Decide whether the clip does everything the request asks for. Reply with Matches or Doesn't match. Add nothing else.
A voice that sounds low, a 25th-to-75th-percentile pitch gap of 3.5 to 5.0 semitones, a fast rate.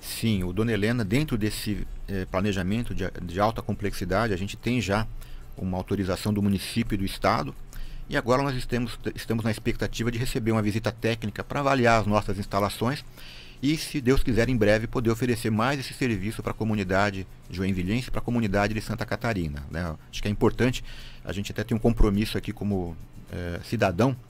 Doesn't match